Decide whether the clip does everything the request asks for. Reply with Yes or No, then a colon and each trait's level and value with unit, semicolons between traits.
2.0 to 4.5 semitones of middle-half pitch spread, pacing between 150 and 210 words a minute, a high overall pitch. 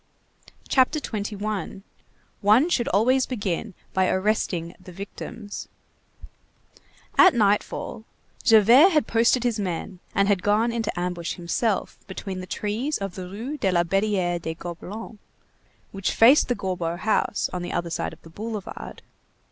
No: average, 3.8 semitones; average, 140 wpm; high, 205 Hz